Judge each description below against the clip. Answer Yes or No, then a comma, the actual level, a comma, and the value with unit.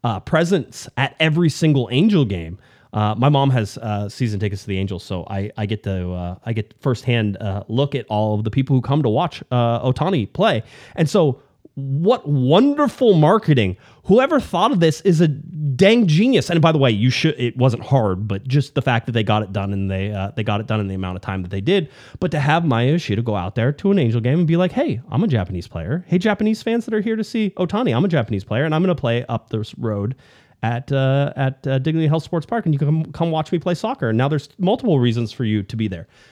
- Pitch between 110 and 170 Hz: Yes, low, 135 Hz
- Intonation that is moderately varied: No, wide, 7.0 semitones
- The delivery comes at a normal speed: No, fast, 255 wpm